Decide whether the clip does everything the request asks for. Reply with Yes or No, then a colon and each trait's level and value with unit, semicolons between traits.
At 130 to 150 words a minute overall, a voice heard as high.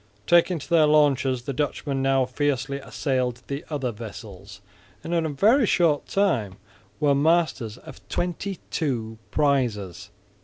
No: average, 140 wpm; medium, 140 Hz